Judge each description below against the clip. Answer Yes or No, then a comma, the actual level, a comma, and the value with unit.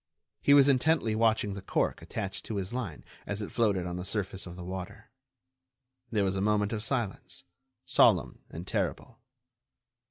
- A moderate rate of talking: Yes, average, 160 wpm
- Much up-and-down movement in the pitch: No, average, 3.2 semitones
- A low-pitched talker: Yes, low, 105 Hz